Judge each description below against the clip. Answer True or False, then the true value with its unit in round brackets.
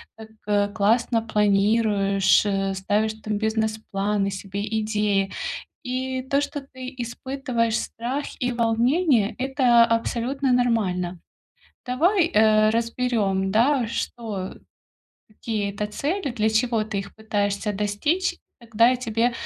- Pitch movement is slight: False (3.3 semitones)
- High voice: True (220 Hz)